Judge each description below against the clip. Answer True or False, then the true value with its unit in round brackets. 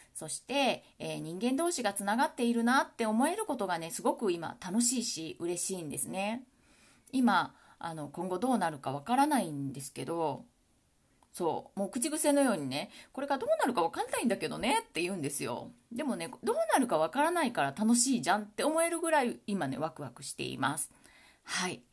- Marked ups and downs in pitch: True (8.9 semitones)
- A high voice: True (230 Hz)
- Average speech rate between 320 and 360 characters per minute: False (385 characters per minute)